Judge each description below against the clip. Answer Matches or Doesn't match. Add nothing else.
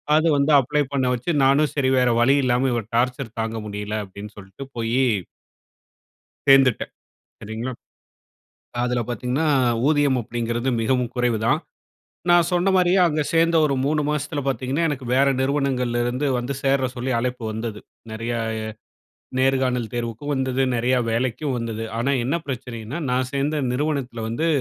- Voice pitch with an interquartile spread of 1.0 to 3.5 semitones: Matches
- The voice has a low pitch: Matches